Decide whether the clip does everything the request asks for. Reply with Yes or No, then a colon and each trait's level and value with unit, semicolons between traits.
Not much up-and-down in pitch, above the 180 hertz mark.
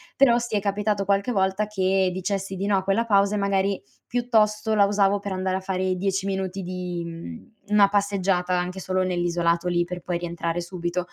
Yes: narrow, 1.9 semitones; high, 190 Hz